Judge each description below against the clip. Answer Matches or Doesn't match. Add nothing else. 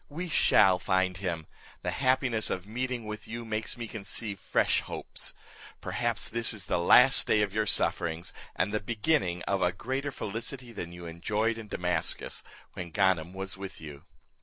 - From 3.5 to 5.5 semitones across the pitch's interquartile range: Matches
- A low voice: Matches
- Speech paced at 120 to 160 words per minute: Doesn't match